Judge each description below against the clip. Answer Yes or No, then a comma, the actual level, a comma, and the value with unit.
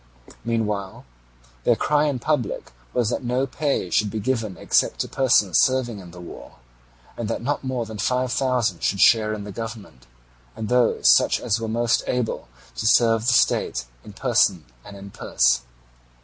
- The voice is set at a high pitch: No, low, 115 Hz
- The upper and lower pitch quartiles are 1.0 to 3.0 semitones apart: No, average, 3.4 semitones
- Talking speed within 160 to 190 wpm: Yes, average, 175 wpm